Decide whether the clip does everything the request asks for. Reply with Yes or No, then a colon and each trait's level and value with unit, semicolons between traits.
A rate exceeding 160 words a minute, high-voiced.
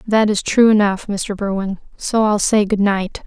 Yes: average, 200 wpm; high, 205 Hz